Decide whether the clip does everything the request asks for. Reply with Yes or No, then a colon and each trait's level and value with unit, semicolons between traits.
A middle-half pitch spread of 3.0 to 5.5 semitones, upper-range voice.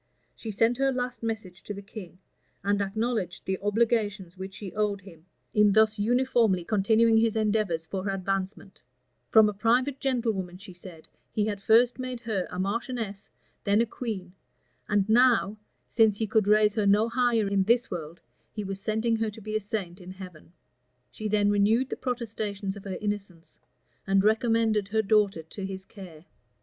No: narrow, 2.6 semitones; high, 210 Hz